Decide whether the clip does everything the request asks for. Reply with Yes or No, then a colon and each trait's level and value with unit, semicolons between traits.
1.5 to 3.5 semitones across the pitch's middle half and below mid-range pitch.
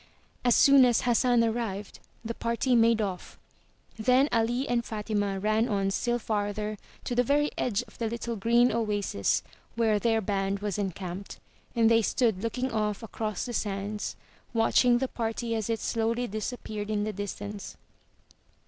No: narrow, 2.6 semitones; high, 225 Hz